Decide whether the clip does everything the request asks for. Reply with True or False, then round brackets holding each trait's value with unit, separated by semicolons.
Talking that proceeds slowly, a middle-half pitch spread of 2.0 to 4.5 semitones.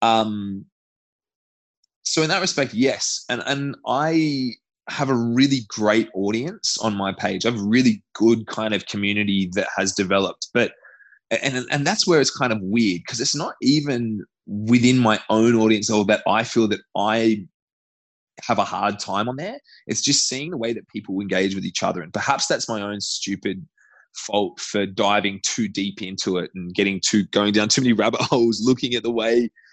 False (185 wpm; 3.7 semitones)